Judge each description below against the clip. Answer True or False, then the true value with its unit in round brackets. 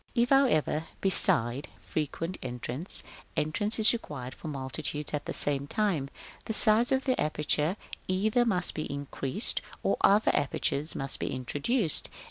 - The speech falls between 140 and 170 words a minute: True (150 wpm)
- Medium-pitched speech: True (155 Hz)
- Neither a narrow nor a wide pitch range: False (7.1 semitones)